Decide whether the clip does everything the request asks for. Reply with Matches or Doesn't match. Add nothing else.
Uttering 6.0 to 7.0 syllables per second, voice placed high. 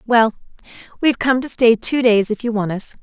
Doesn't match